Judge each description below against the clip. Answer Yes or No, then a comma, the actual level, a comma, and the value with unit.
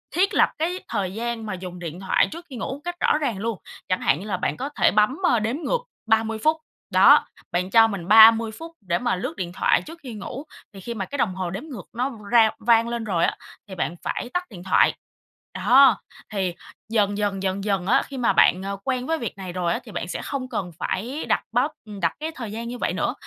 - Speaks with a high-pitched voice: Yes, high, 220 Hz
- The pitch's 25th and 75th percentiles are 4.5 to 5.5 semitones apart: Yes, average, 5.0 semitones